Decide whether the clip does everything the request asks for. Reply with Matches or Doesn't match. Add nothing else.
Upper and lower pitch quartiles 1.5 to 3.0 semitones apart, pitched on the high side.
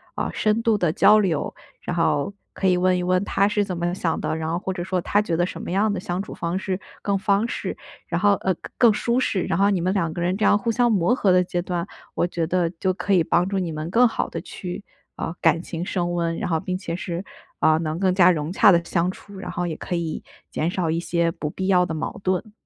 Doesn't match